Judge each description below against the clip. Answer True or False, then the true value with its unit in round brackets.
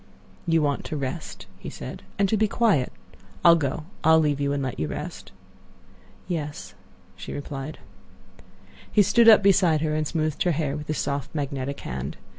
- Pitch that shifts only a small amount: False (3.2 semitones)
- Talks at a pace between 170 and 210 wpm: True (175 wpm)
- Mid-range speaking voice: True (150 Hz)